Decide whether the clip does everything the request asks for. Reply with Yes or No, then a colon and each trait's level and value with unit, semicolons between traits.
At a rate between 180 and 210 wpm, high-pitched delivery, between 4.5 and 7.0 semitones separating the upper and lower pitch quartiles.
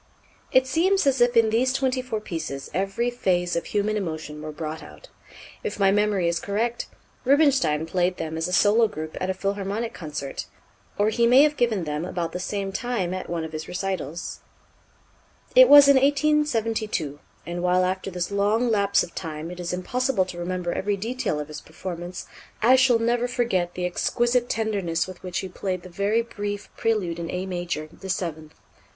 Yes: average, 185 wpm; high, 195 Hz; average, 5.2 semitones